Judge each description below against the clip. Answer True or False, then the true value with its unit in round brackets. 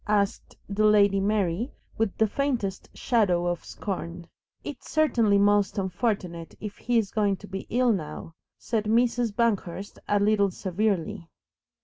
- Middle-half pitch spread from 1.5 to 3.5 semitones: True (2.8 semitones)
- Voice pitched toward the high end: True (205 Hz)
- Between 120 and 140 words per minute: True (135 wpm)